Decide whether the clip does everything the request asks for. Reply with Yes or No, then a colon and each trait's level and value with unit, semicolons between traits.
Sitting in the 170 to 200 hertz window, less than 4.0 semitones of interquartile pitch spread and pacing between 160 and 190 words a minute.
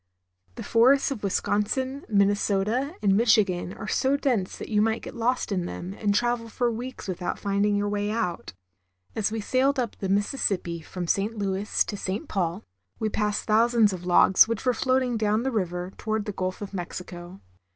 No: high, 210 Hz; average, 3.3 semitones; average, 185 wpm